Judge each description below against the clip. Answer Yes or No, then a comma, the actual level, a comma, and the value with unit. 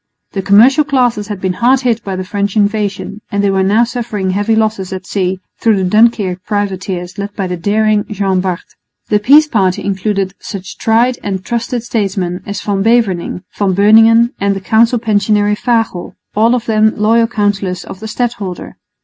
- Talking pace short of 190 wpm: Yes, average, 180 wpm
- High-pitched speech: Yes, high, 205 Hz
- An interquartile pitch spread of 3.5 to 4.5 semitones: No, average, 2.9 semitones